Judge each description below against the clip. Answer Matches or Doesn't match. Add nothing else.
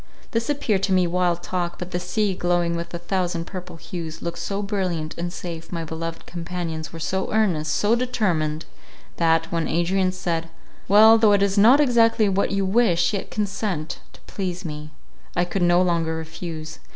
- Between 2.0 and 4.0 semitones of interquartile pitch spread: Matches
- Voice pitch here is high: Doesn't match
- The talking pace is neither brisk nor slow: Matches